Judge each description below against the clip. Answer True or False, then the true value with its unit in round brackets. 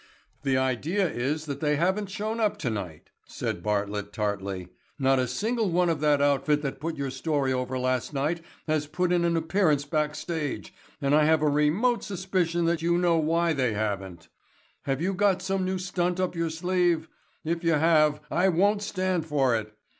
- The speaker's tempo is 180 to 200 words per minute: True (185 wpm)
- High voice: False (155 Hz)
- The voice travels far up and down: False (4.8 semitones)